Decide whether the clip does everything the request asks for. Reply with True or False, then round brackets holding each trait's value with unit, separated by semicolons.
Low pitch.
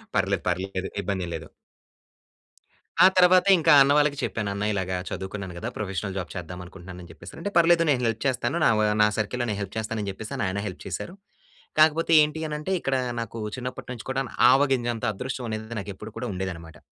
True (110 Hz)